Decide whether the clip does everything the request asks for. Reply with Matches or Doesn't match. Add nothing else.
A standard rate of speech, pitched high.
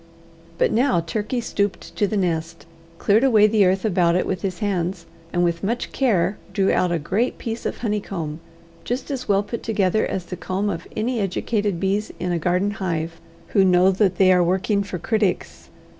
Matches